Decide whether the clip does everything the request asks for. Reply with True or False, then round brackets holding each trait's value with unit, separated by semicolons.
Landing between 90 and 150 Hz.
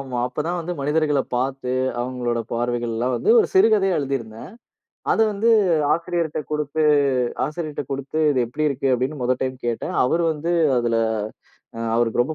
True (135 Hz)